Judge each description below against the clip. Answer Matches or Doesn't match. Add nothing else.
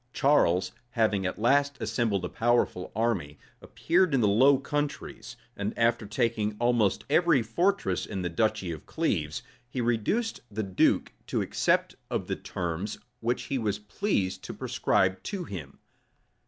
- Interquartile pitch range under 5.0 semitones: Doesn't match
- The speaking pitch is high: Doesn't match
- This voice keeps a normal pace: Matches